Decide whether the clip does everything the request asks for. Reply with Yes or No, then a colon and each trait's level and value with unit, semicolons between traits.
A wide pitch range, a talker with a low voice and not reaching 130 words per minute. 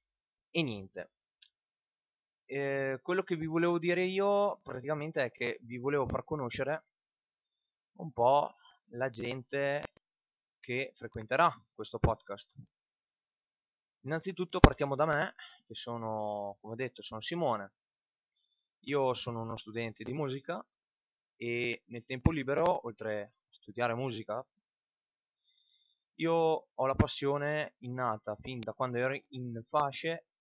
No: average, 4.8 semitones; low, 130 Hz; average, 120 wpm